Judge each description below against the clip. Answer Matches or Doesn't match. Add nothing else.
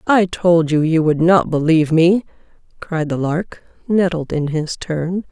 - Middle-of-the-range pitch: Matches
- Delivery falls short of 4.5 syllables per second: Matches